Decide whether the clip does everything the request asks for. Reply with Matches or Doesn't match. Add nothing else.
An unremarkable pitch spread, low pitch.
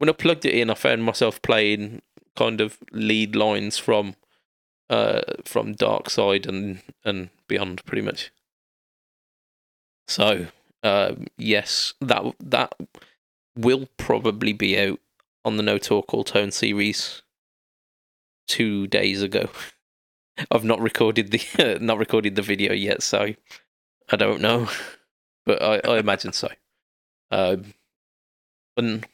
Doesn't match